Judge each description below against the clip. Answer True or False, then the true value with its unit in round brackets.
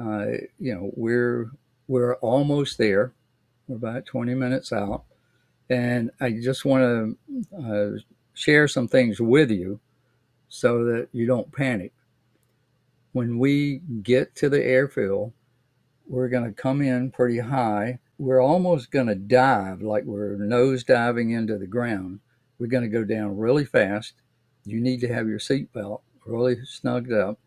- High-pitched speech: False (125 Hz)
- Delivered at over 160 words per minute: False (150 wpm)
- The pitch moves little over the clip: True (2.1 semitones)